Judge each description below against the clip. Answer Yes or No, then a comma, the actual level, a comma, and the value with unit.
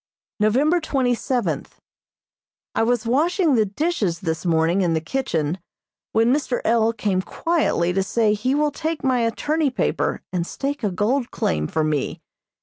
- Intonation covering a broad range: Yes, wide, 7.0 semitones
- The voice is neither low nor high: No, high, 230 Hz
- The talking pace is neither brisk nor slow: Yes, average, 155 wpm